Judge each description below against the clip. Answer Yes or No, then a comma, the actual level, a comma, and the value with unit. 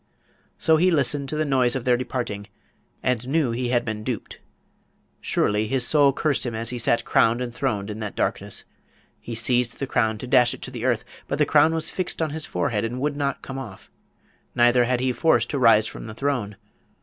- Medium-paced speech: No, fast, 215 wpm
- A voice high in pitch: No, low, 125 Hz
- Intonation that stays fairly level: No, average, 3.4 semitones